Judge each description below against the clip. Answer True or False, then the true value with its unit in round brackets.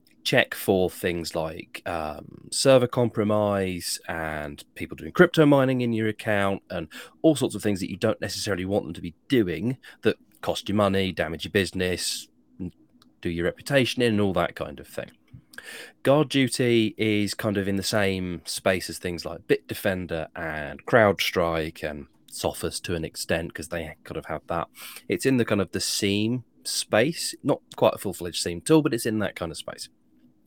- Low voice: True (100 Hz)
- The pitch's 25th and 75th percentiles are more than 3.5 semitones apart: True (5.0 semitones)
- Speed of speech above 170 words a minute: True (185 wpm)